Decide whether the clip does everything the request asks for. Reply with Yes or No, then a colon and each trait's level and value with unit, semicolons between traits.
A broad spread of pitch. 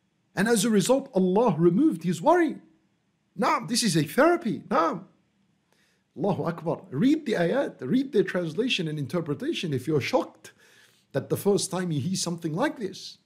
Yes: wide, 5.7 semitones